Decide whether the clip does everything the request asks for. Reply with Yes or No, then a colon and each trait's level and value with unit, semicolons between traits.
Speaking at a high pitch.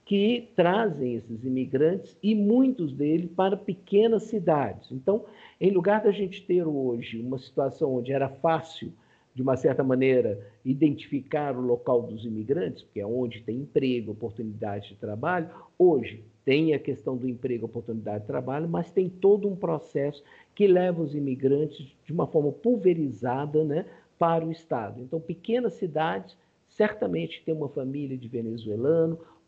No: medium, 150 Hz